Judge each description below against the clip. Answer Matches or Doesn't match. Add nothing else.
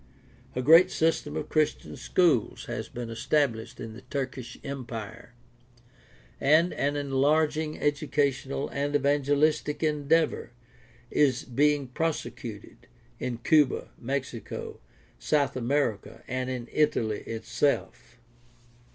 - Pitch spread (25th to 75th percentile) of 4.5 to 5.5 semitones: Doesn't match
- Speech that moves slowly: Matches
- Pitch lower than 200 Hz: Matches